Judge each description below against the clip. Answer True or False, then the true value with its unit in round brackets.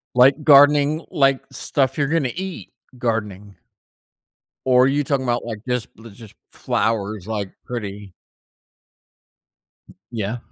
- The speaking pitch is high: False (125 Hz)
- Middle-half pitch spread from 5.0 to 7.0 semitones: False (4.6 semitones)